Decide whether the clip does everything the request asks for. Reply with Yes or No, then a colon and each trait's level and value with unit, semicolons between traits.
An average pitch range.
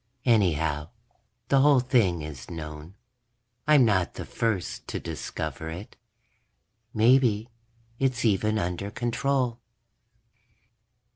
No: wide, 6.5 semitones